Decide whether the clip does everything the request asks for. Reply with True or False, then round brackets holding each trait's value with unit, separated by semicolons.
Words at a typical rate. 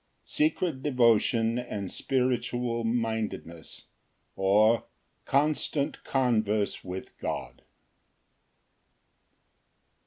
False (60 wpm)